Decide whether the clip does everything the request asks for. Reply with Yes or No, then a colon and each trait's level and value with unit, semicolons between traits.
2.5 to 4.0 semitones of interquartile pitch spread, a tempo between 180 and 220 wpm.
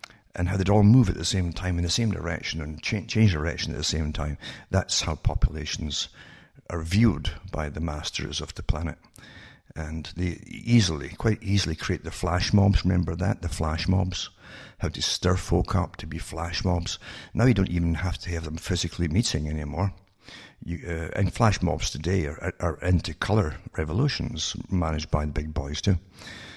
Yes: average, 3.4 semitones; average, 190 wpm